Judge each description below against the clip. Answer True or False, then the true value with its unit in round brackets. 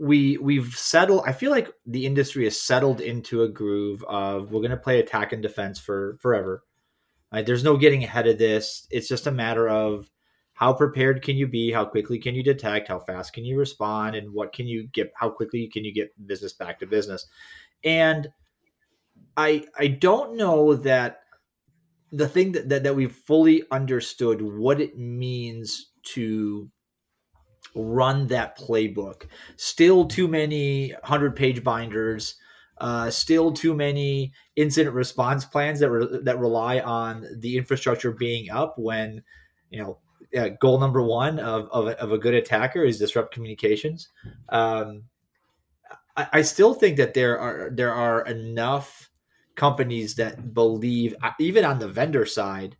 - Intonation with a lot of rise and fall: False (4.2 semitones)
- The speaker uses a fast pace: False (160 wpm)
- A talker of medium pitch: False (125 Hz)